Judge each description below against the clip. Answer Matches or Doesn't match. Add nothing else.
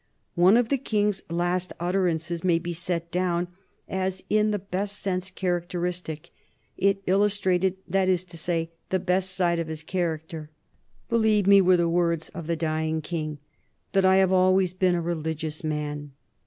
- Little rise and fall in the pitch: Matches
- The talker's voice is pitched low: Doesn't match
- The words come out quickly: Doesn't match